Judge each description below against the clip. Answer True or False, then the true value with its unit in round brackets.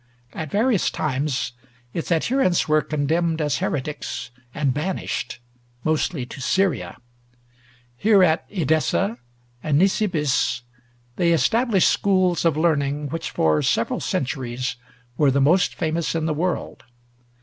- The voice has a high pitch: False (155 Hz)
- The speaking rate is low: True (120 wpm)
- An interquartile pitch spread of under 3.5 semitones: False (4.1 semitones)